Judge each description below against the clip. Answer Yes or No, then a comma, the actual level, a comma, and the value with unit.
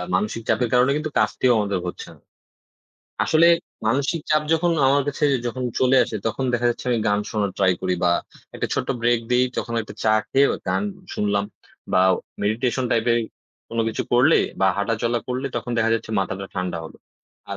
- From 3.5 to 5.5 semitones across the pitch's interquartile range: Yes, average, 3.9 semitones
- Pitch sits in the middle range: No, low, 120 Hz